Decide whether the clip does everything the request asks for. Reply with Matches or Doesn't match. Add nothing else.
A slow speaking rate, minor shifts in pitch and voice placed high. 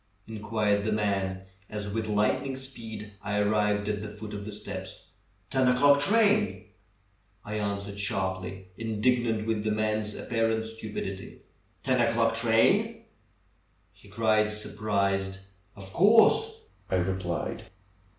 Doesn't match